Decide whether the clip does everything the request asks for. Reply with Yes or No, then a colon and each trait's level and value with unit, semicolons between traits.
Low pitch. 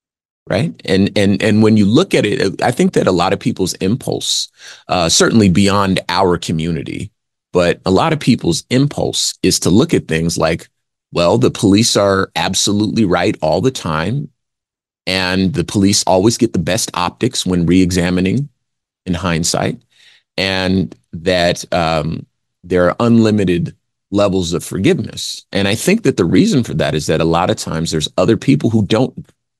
Yes: very low, 95 Hz